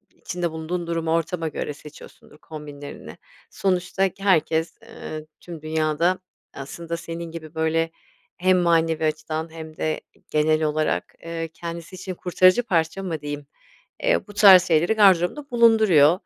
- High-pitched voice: No, medium, 165 Hz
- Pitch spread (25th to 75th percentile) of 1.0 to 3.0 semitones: Yes, narrow, 2.5 semitones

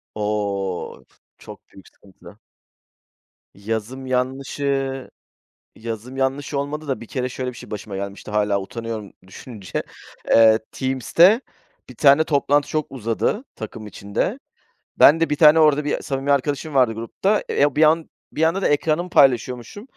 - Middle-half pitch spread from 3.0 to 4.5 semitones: No, average, 5.0 semitones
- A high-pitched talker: No, low, 130 Hz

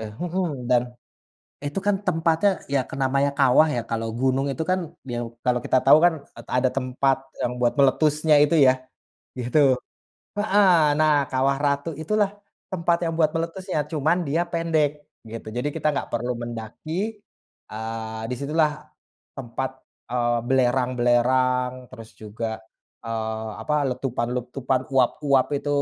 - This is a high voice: No, low, 130 Hz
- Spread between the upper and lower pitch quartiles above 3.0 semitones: Yes, average, 4.2 semitones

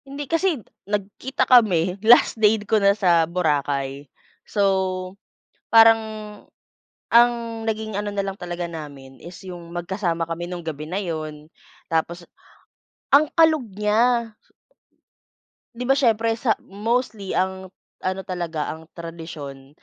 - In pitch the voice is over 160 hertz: Yes, high, 190 Hz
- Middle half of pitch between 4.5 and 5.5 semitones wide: Yes, average, 5.0 semitones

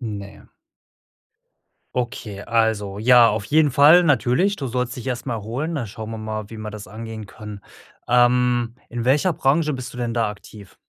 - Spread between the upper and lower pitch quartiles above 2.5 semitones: Yes, average, 2.9 semitones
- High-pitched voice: No, low, 120 Hz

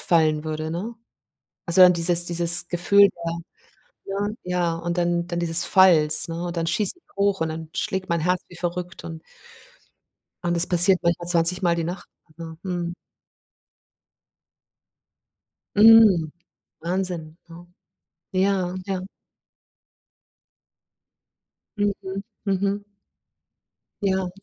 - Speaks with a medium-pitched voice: Yes, medium, 175 Hz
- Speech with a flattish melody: Yes, narrow, 2.1 semitones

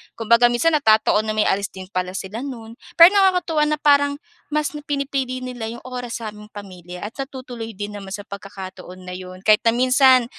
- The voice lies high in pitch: Yes, high, 230 Hz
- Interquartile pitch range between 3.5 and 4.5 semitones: No, average, 4.9 semitones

